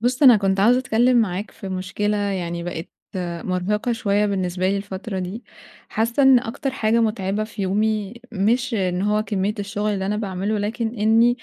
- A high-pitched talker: Yes, high, 210 Hz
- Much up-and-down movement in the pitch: No, average, 2.9 semitones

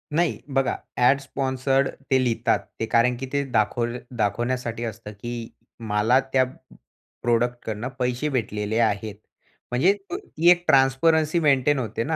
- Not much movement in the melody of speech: No, average, 3.1 semitones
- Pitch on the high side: No, low, 125 Hz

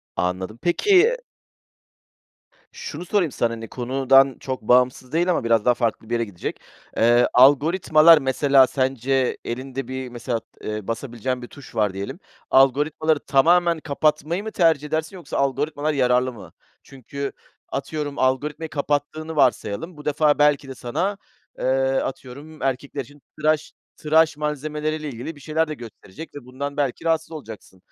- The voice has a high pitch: No, medium, 140 Hz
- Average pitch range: Yes, average, 3.7 semitones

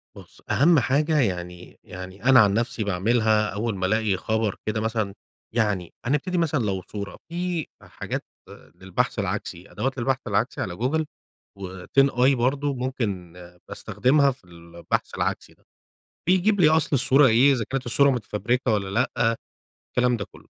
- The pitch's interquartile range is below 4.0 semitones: No, average, 5.2 semitones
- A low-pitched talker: Yes, low, 115 Hz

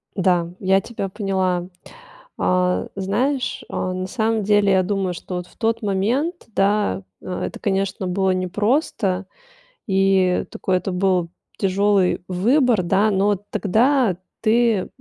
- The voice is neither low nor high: No, high, 195 Hz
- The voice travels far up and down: No, narrow, 2.6 semitones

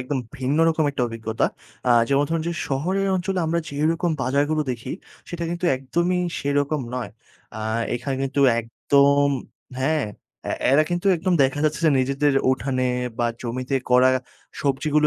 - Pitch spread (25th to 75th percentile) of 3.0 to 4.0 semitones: Yes, average, 3.4 semitones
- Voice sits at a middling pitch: Yes, medium, 145 Hz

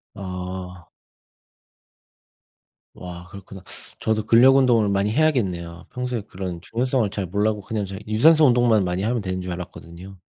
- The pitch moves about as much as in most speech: Yes, average, 4.2 semitones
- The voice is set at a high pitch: No, low, 100 Hz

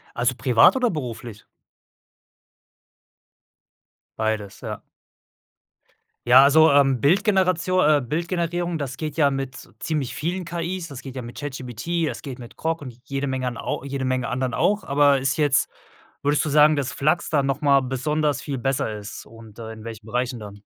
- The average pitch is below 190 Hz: Yes, medium, 140 Hz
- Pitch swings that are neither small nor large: Yes, average, 4.0 semitones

